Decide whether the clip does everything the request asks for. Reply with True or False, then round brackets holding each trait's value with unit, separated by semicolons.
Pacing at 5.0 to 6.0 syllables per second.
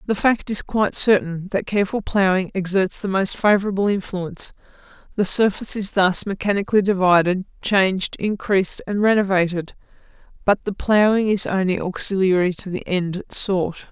True (5.3 syllables/s)